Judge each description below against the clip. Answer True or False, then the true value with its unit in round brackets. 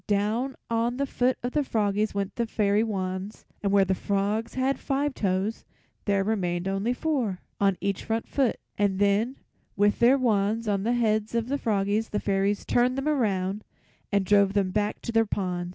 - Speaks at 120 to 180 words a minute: False (195 wpm)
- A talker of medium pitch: False (210 Hz)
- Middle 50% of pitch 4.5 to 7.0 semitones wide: False (3.0 semitones)